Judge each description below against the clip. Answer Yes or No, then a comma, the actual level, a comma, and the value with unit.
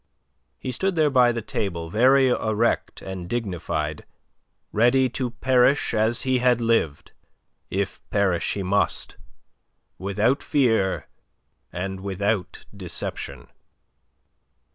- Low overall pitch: Yes, low, 110 Hz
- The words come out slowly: Yes, slow, 105 wpm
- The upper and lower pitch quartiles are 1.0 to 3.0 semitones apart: No, average, 4.8 semitones